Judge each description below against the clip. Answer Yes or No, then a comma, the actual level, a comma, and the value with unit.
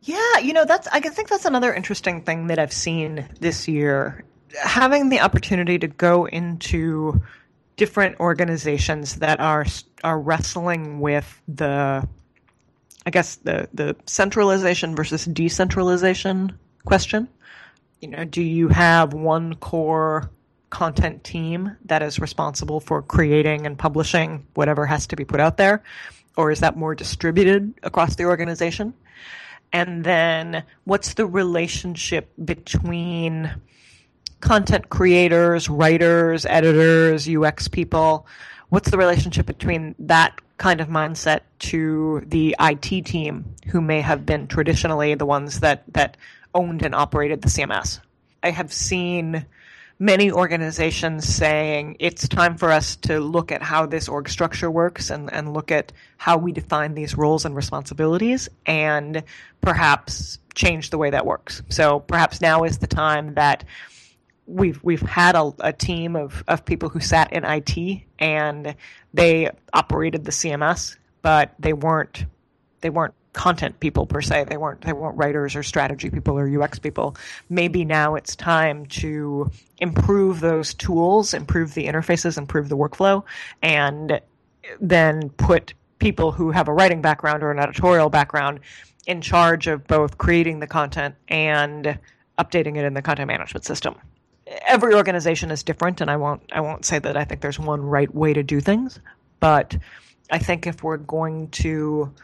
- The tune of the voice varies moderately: No, narrow, 2.3 semitones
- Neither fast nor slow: Yes, average, 150 wpm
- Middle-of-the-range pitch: Yes, medium, 160 Hz